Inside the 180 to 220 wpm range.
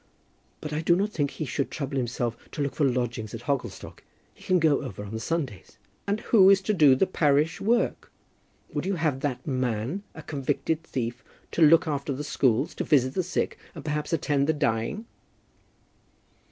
Yes: average, 190 wpm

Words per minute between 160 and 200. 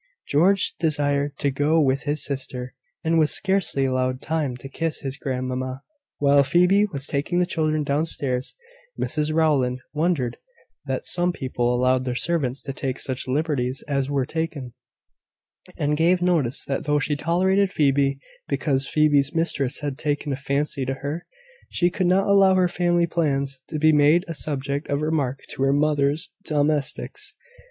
Yes: average, 165 wpm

